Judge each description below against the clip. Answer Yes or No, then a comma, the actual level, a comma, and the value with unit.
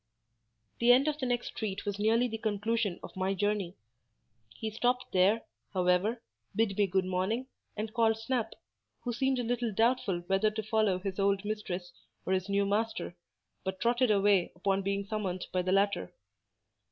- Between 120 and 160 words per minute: No, average, 170 wpm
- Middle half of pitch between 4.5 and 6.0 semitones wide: No, average, 2.9 semitones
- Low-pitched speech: No, high, 205 Hz